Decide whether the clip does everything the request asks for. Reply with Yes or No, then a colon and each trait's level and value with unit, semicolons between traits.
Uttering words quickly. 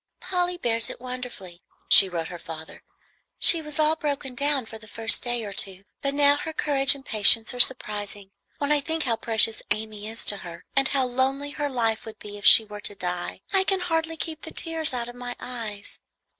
Yes: fast, 210 wpm